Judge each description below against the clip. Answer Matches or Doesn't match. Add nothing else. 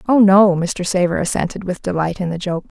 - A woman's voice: Matches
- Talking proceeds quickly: Matches